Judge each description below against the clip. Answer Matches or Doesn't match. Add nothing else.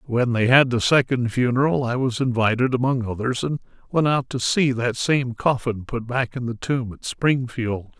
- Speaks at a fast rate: Doesn't match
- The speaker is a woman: Doesn't match